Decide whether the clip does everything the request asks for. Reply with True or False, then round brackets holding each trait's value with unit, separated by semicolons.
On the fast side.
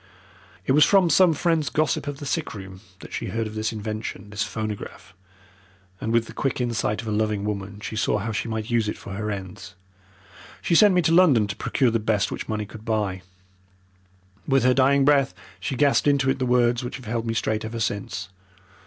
True (215 wpm)